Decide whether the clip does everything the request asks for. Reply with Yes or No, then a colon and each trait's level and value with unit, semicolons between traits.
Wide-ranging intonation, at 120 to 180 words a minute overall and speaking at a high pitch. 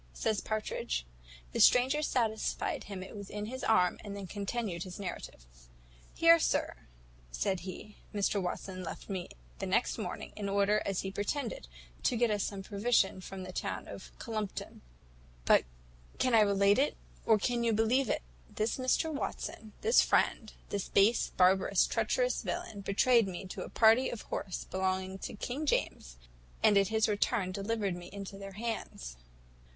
No: average, 3.1 semitones; average, 165 wpm; high, 205 Hz